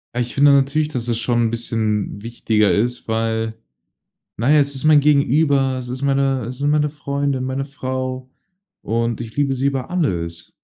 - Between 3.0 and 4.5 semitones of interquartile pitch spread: Yes, average, 3.3 semitones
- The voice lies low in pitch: Yes, low, 130 Hz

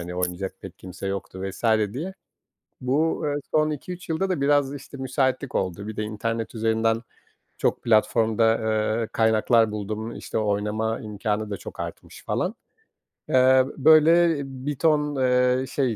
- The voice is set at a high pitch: No, low, 115 Hz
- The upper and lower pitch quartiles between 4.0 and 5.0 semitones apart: Yes, average, 4.5 semitones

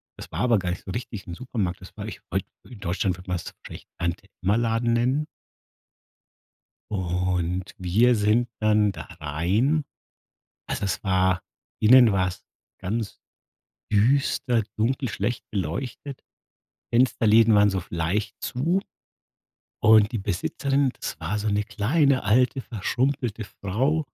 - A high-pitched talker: No, low, 105 Hz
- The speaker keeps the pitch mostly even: No, average, 4.7 semitones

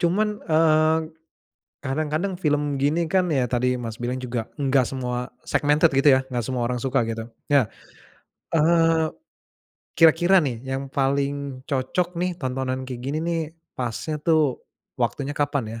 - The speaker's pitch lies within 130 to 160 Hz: Yes, medium, 140 Hz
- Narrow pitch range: No, average, 3.9 semitones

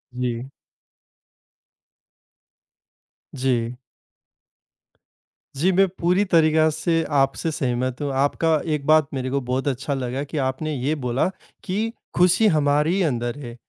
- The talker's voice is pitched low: No, medium, 145 Hz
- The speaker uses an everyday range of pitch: Yes, average, 3.8 semitones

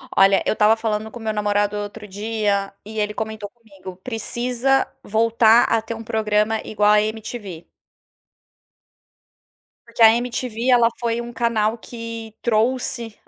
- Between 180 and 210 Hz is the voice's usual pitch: No, high, 220 Hz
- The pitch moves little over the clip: Yes, narrow, 1.7 semitones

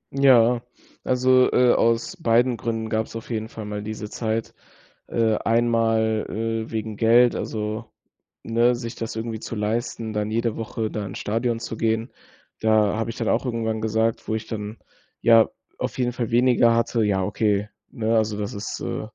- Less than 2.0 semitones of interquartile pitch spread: Yes, narrow, 1.2 semitones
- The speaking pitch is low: Yes, low, 115 Hz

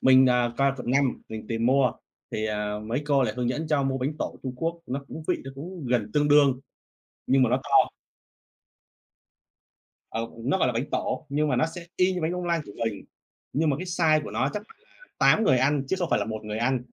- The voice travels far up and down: No, average, 4.2 semitones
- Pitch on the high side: No, low, 135 Hz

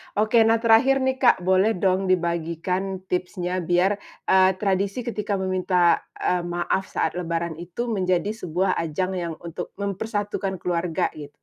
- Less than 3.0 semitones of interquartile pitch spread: Yes, narrow, 2.6 semitones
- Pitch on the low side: No, medium, 185 Hz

